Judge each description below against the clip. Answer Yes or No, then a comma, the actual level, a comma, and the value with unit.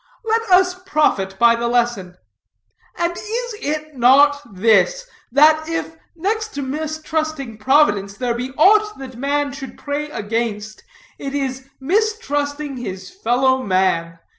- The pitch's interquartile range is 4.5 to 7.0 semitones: Yes, average, 5.2 semitones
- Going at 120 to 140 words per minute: Yes, slow, 135 wpm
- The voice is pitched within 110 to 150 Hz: No, very high, 280 Hz